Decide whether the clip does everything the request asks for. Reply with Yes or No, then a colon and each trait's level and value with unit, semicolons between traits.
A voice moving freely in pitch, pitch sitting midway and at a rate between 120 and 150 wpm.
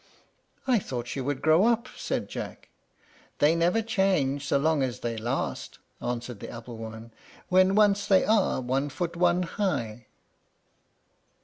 Yes: wide, 7.6 semitones; medium, 145 Hz; average, 145 wpm